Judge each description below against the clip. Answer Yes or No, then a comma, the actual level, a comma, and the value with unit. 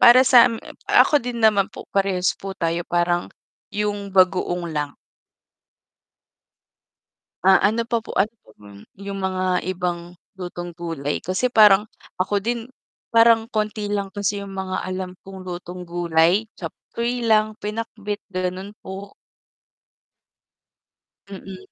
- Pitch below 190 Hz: No, high, 195 Hz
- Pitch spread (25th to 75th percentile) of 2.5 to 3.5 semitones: Yes, average, 2.8 semitones